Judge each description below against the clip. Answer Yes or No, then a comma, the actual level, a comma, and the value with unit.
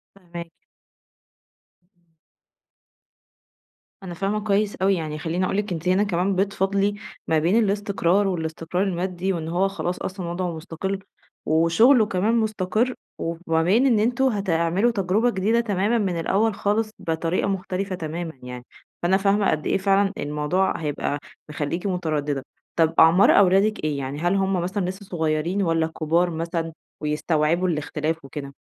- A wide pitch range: No, average, 3.4 semitones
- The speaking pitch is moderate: Yes, medium, 180 Hz